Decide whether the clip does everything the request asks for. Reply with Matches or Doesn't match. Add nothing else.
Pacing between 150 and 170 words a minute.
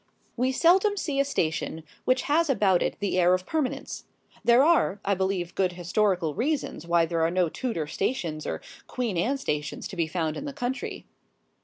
Doesn't match